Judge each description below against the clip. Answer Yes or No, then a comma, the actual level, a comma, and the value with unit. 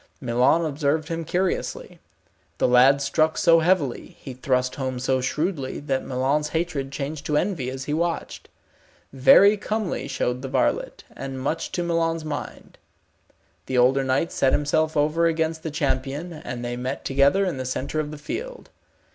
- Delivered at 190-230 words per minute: No, average, 165 wpm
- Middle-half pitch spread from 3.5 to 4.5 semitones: Yes, average, 3.8 semitones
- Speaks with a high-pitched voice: No, medium, 145 Hz